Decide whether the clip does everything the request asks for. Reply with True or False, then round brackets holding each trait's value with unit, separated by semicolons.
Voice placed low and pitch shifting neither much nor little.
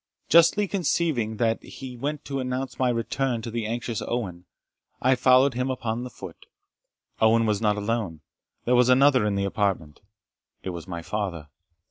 True (115 Hz; 3.8 semitones)